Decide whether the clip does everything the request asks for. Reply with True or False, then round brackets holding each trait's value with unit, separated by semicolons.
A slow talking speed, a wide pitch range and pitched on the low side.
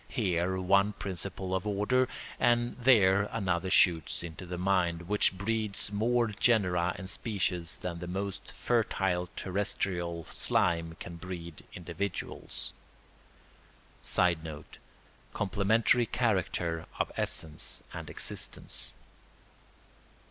False (100 wpm; 3.0 semitones; 95 Hz)